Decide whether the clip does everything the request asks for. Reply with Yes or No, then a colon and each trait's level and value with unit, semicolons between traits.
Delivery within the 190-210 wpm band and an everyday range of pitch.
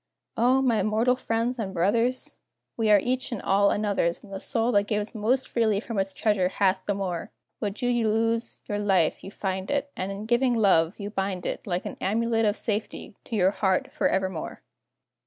Yes: average, 195 wpm; average, 3.1 semitones